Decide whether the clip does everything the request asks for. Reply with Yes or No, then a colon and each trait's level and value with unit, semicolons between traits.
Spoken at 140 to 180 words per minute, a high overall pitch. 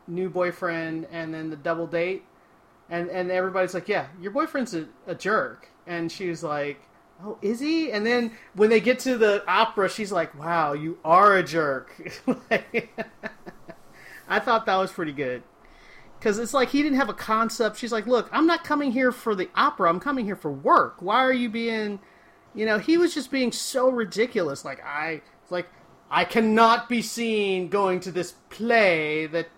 No: average, 190 wpm; high, 205 Hz